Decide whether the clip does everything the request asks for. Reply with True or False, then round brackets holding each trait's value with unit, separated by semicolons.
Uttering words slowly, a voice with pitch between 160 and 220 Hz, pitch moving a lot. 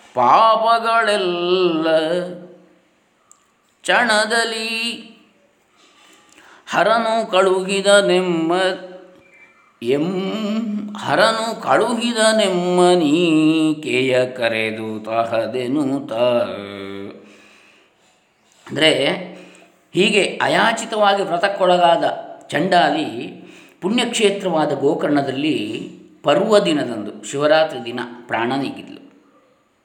True (45 wpm; 185 Hz; 6.2 semitones)